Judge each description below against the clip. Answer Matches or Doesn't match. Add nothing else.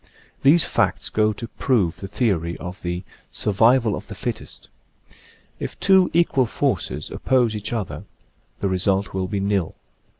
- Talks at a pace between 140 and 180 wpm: Matches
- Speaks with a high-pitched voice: Doesn't match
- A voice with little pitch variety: Doesn't match